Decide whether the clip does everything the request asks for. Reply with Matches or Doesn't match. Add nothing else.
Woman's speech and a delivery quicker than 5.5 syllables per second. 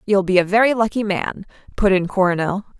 Matches